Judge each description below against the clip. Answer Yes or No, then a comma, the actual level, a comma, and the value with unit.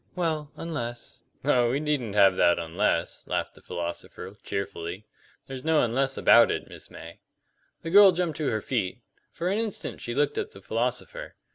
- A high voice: No, low, 135 Hz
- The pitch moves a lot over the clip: Yes, wide, 7.7 semitones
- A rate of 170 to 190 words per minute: Yes, average, 175 wpm